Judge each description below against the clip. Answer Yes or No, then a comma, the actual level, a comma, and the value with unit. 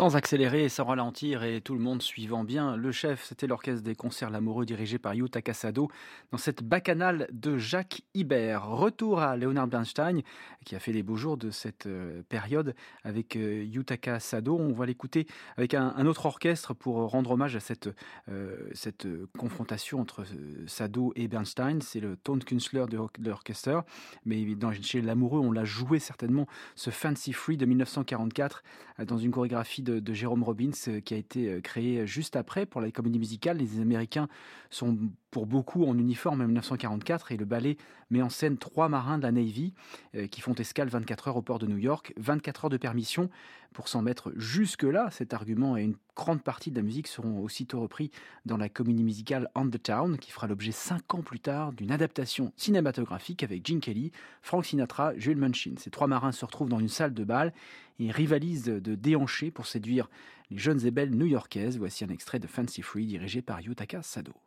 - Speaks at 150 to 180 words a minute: No, average, 195 wpm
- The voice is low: Yes, low, 125 Hz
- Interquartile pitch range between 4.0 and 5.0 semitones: Yes, average, 4.3 semitones